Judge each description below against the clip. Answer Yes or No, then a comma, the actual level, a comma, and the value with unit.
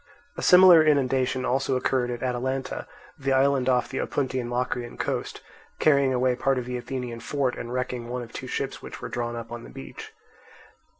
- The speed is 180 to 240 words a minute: Yes, average, 185 wpm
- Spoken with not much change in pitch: Yes, narrow, 1.6 semitones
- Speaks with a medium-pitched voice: No, low, 125 Hz